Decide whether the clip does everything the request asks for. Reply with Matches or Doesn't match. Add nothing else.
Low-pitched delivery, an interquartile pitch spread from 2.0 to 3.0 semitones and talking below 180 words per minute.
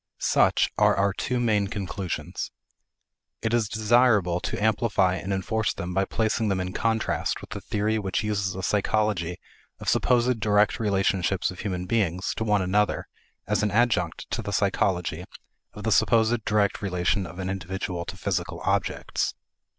Matches